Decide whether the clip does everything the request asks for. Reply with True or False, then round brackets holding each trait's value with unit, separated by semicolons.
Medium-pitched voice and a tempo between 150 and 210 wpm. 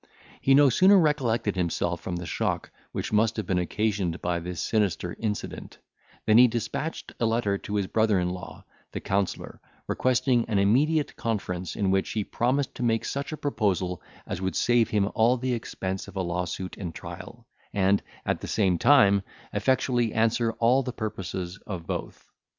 False (105 Hz; 175 wpm)